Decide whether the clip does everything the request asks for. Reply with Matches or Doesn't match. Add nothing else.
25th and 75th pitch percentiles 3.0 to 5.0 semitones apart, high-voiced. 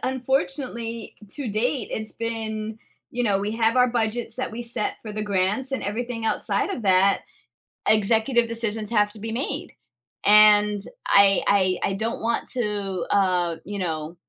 Doesn't match